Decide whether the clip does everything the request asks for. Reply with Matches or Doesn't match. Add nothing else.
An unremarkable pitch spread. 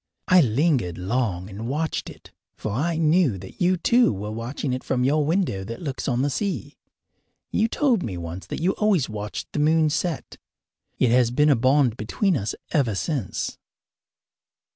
Doesn't match